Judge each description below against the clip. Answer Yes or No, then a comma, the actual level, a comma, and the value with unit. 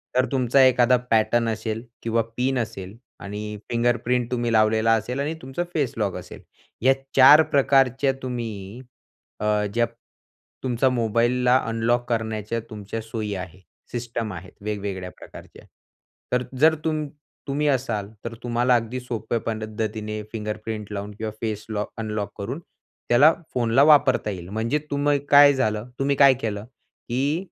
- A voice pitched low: Yes, low, 115 Hz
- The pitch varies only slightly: No, average, 3.1 semitones